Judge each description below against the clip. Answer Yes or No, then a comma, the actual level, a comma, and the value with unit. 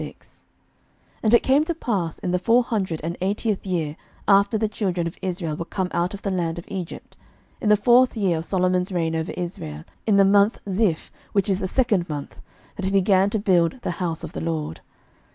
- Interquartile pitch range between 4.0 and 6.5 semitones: No, average, 3.3 semitones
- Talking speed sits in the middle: No, fast, 210 wpm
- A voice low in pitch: No, high, 190 Hz